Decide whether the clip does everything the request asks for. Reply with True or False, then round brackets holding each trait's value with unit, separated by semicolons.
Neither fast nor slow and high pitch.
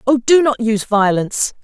True (185 wpm; 235 Hz)